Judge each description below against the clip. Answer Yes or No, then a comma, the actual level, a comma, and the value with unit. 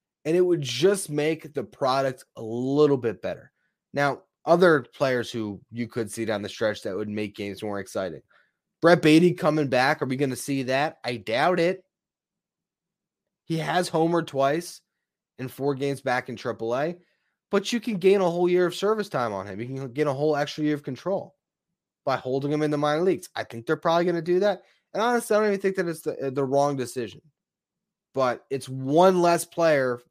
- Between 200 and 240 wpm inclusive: Yes, fast, 205 wpm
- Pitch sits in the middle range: Yes, medium, 150 Hz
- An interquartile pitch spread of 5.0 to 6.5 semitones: Yes, wide, 5.4 semitones